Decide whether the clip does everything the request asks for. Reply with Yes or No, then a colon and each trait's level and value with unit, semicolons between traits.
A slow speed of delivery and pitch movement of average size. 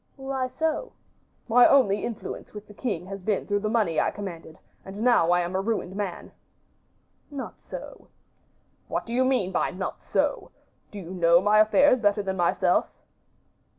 No: average, 170 wpm; average, 4.5 semitones